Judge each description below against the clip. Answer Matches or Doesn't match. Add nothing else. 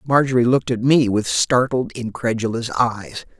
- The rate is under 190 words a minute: Matches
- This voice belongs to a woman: Doesn't match